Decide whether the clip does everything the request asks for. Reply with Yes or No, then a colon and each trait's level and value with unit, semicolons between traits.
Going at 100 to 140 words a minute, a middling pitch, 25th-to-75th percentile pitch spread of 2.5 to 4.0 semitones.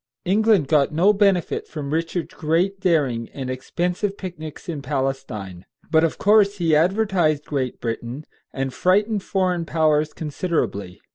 No: slow, 135 wpm; medium, 160 Hz; average, 5.2 semitones